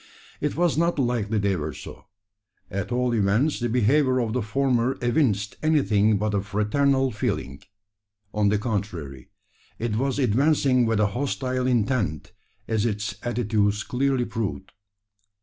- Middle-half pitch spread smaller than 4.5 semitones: Yes, average, 4.1 semitones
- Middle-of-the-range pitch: No, low, 115 Hz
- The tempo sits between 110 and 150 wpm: Yes, average, 140 wpm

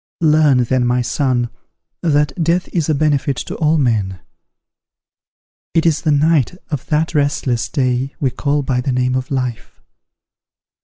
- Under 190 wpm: Yes, average, 150 wpm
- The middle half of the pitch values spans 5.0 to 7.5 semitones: No, average, 3.3 semitones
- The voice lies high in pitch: No, medium, 140 Hz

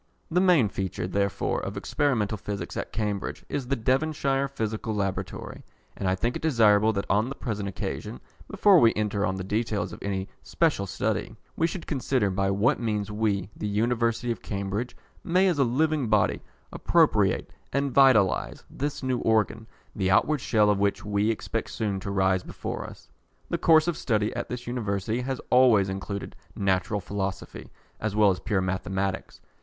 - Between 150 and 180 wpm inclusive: Yes, average, 170 wpm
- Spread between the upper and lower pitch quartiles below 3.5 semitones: No, average, 4.4 semitones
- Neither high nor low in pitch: No, low, 110 Hz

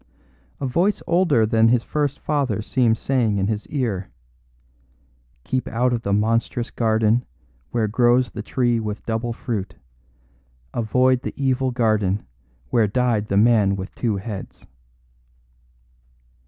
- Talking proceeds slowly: Yes, slow, 130 wpm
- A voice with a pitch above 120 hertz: No, low, 115 Hz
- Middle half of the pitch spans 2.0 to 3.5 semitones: Yes, average, 3.0 semitones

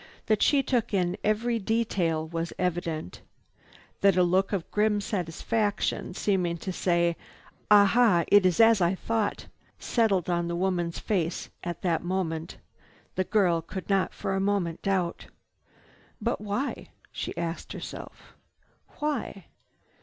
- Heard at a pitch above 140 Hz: Yes, high, 190 Hz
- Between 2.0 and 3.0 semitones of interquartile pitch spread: No, average, 3.4 semitones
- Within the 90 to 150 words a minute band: Yes, average, 140 wpm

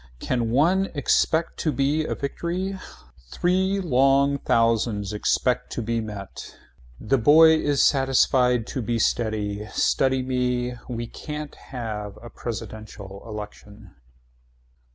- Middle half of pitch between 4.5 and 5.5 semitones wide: Yes, average, 4.8 semitones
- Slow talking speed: Yes, slow, 120 wpm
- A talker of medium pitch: No, low, 125 Hz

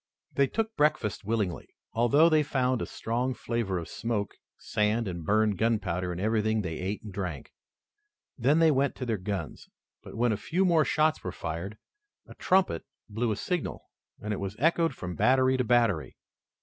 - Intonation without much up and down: No, average, 5.1 semitones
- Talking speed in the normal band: Yes, average, 175 wpm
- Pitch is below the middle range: Yes, low, 115 Hz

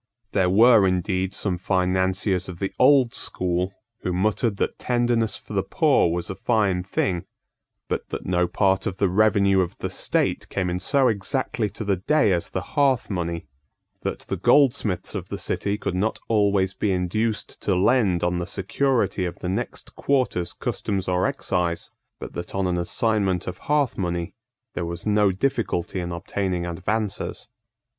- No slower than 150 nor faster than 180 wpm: Yes, average, 170 wpm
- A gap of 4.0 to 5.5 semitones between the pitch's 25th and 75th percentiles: No, average, 3.2 semitones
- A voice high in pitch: No, very low, 95 Hz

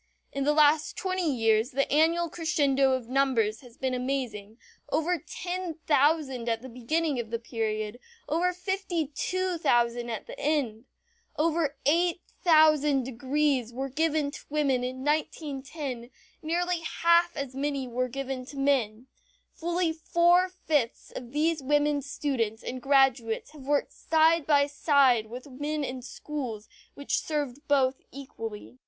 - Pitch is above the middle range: Yes, very high, 280 Hz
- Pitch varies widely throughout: No, average, 3.9 semitones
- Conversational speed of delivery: Yes, average, 145 wpm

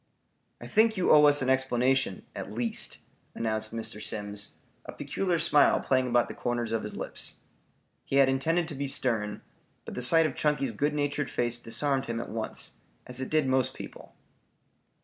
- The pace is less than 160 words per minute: No, average, 180 wpm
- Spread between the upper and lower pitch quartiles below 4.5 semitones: Yes, average, 4.0 semitones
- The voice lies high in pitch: No, low, 130 Hz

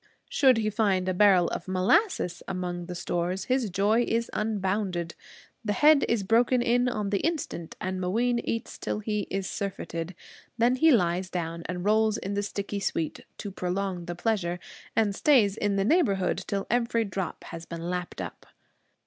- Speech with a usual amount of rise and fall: Yes, average, 3.8 semitones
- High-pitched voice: Yes, high, 200 Hz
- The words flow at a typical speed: Yes, average, 175 wpm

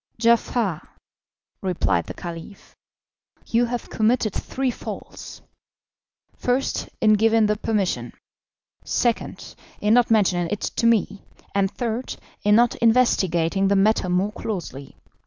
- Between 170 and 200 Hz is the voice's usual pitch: No, high, 215 Hz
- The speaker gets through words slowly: Yes, slow, 120 wpm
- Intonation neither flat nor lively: Yes, average, 3.3 semitones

